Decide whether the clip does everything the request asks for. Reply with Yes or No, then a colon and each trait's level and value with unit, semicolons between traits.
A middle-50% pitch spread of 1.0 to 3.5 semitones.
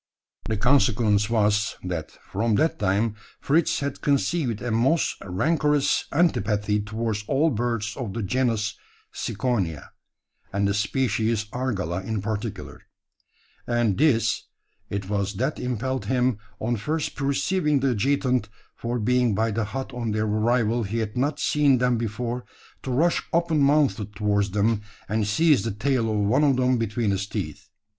No: average, 4.0 semitones